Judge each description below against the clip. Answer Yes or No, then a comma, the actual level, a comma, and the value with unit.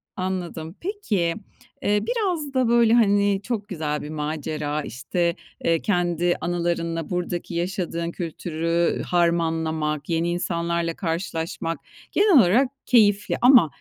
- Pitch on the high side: No, medium, 175 Hz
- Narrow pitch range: No, average, 3.7 semitones